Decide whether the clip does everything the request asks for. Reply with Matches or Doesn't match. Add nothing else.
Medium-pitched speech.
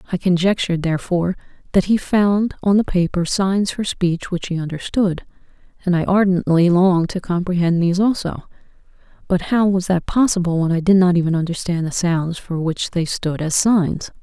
Matches